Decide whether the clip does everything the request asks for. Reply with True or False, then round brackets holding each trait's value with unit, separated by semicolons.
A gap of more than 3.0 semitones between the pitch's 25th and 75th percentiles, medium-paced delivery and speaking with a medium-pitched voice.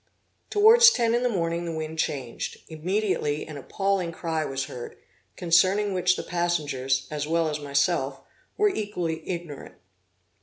True (4.6 semitones; 145 wpm; 170 Hz)